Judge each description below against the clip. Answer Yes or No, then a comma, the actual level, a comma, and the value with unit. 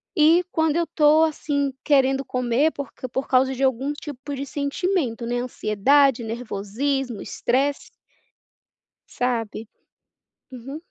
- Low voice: No, very high, 270 Hz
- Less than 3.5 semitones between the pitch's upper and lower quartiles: Yes, average, 2.9 semitones